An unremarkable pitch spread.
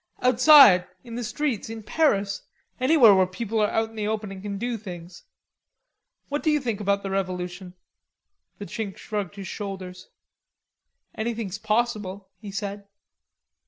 Yes: average, 3.0 semitones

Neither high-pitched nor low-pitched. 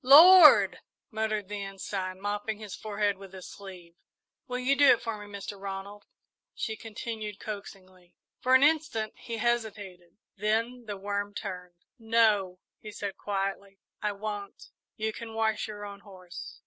No: high, 205 Hz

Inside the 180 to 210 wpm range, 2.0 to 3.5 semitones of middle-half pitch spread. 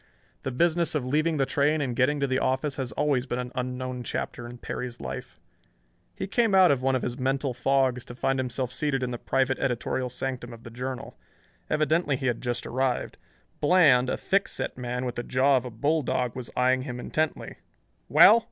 Yes: average, 200 wpm; narrow, 2.5 semitones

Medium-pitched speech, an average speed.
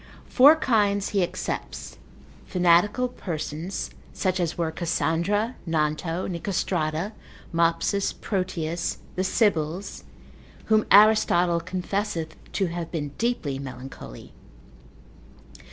No: medium, 175 Hz; slow, 90 wpm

